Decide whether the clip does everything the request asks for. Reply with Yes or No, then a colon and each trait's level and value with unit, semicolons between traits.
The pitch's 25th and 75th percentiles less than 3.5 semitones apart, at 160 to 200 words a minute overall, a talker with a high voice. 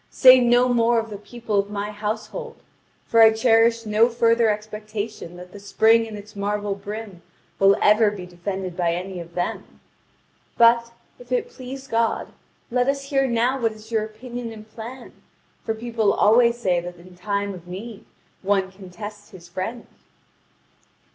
Yes: average, 2.8 semitones; average, 165 wpm; high, 215 Hz